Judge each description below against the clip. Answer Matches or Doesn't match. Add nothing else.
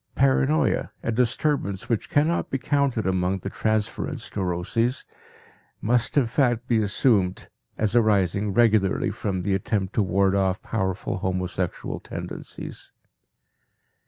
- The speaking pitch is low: Matches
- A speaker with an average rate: Doesn't match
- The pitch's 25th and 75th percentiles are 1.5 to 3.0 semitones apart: Doesn't match